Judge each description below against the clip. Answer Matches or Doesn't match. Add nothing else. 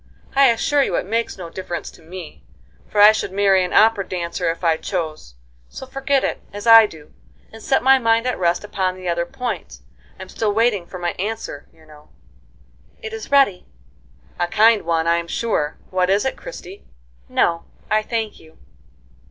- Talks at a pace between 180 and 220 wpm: Matches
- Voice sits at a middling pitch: Doesn't match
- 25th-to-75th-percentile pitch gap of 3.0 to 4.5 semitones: Doesn't match